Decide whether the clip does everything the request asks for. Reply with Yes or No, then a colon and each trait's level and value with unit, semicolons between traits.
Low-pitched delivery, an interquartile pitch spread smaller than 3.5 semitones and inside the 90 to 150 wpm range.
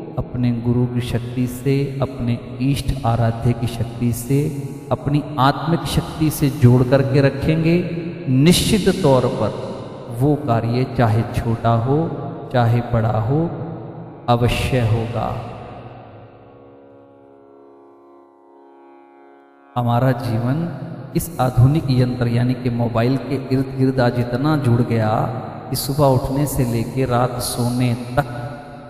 Yes: low, 125 Hz; average, 2.9 semitones; slow, 110 wpm